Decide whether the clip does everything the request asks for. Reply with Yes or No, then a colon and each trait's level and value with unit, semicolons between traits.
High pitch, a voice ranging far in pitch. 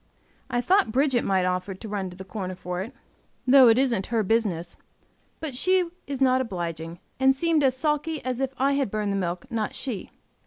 Yes: high, 230 Hz; wide, 6.1 semitones